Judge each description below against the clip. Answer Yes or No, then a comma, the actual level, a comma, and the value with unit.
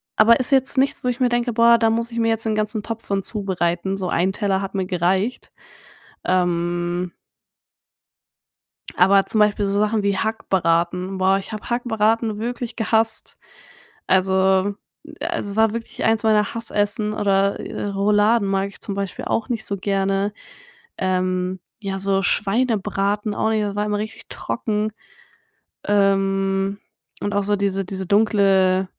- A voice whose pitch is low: No, high, 200 Hz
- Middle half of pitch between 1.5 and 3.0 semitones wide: Yes, narrow, 2.4 semitones